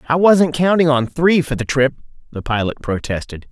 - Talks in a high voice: No, medium, 145 Hz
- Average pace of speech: Yes, average, 190 wpm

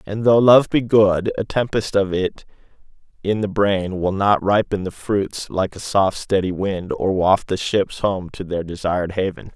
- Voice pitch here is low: Yes, low, 100 Hz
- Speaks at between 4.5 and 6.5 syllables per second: No, 4.3 syllables/s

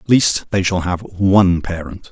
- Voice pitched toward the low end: Yes, very low, 95 Hz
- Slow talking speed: No, average, 200 wpm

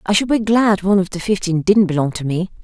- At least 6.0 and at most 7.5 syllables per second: Yes, 6.2 syllables/s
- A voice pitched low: No, high, 190 Hz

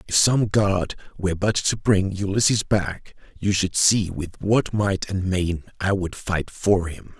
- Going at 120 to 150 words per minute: No, average, 185 wpm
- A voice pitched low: Yes, very low, 95 Hz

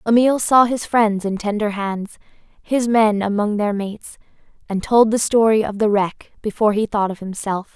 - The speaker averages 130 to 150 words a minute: No, average, 185 wpm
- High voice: Yes, high, 215 Hz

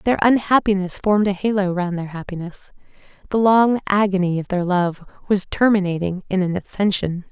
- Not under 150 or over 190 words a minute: Yes, average, 155 wpm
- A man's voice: No, female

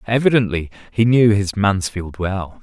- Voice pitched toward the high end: No, low, 100 Hz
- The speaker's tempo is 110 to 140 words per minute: Yes, slow, 135 wpm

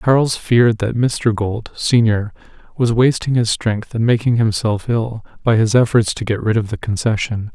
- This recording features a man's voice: Yes, male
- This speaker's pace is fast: No, average, 185 wpm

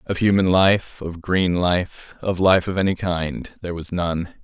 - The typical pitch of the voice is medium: No, very low, 90 Hz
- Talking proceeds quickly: No, average, 190 wpm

